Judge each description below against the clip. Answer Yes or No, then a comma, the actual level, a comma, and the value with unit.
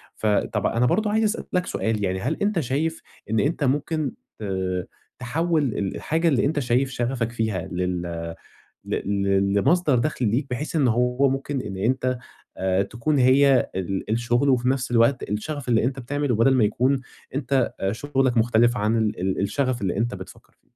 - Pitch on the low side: Yes, low, 125 Hz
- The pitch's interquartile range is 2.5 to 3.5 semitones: No, average, 4.3 semitones